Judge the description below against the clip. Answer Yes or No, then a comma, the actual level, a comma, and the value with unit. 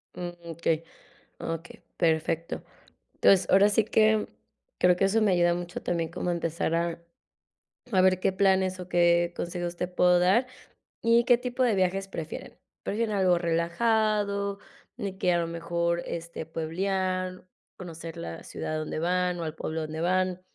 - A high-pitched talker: No, medium, 180 Hz